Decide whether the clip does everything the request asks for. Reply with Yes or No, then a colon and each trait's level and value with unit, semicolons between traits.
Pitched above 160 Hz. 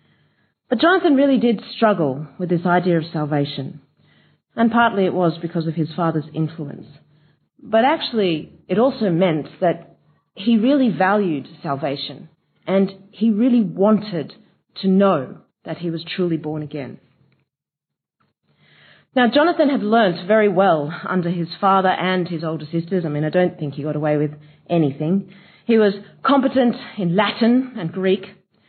Yes: medium, 185 Hz